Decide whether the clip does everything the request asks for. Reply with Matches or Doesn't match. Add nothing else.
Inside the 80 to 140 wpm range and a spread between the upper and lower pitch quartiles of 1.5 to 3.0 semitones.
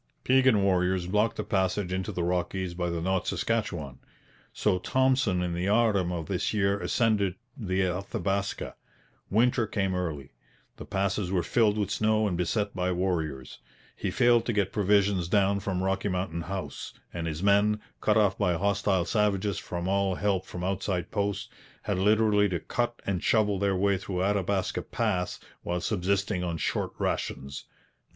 Doesn't match